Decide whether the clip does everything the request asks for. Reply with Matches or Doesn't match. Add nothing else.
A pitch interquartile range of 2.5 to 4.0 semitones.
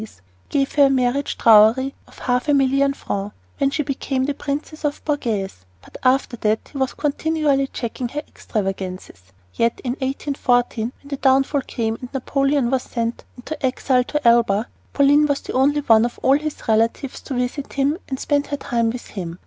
Matches